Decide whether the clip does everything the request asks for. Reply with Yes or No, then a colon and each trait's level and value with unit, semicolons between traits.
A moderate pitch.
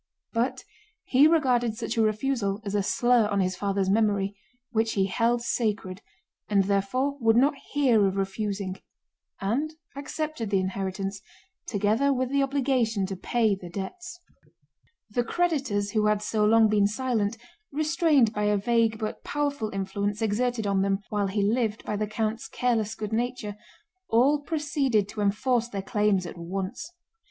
No: high, 220 Hz